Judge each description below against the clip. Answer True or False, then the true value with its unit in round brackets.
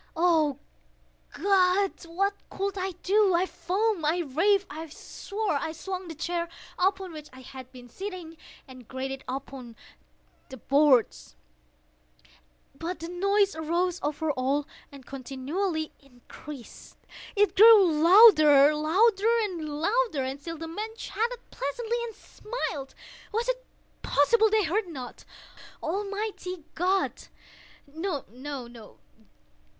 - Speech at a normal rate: False (110 wpm)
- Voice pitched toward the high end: True (335 Hz)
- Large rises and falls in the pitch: True (5.8 semitones)